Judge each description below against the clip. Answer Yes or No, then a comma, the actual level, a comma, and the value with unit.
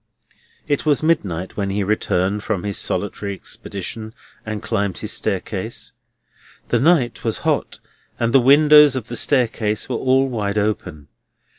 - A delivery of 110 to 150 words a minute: Yes, average, 145 wpm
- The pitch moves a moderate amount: Yes, average, 4.5 semitones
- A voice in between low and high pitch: No, low, 110 Hz